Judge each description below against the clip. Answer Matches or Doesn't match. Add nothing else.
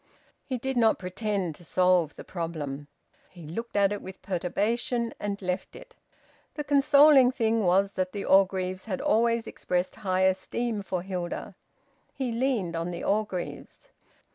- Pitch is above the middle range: Matches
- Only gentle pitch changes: Doesn't match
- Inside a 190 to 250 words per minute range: Doesn't match